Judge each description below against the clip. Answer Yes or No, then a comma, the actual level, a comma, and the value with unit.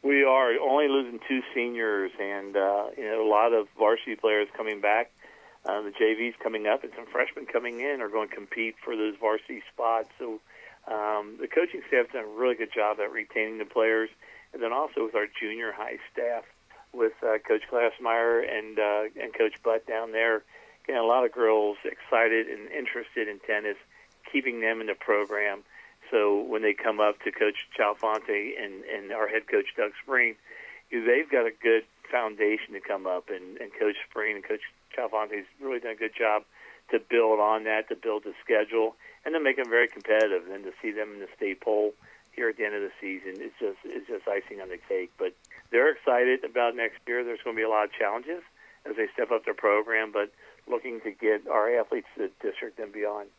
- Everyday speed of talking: No, fast, 210 wpm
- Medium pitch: No, low, 120 Hz